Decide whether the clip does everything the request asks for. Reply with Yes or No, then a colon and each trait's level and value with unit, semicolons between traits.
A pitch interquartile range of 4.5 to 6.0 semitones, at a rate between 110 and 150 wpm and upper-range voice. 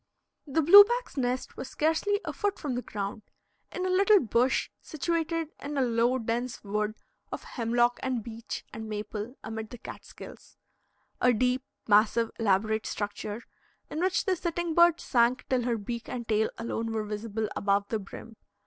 No: wide, 5.6 semitones; average, 165 wpm; high, 240 Hz